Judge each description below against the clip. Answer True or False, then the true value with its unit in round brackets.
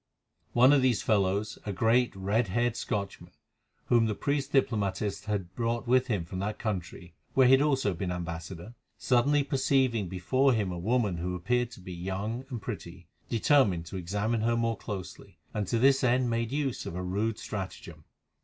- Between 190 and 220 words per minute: False (180 wpm)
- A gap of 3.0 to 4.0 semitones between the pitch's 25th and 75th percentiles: False (4.7 semitones)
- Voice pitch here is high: False (110 Hz)